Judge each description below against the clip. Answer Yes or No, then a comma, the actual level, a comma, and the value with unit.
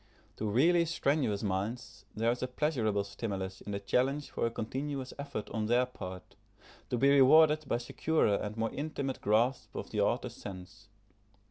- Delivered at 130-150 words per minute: No, average, 165 wpm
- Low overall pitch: Yes, low, 120 Hz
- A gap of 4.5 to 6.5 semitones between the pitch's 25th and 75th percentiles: Yes, average, 5.1 semitones